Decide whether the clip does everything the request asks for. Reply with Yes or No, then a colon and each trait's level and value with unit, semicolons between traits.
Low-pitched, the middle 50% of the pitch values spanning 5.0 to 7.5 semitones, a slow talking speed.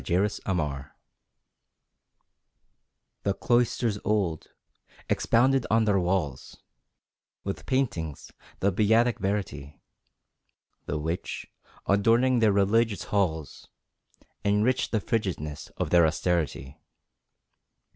Yes: low, 100 Hz; wide, 5.6 semitones; slow, 90 wpm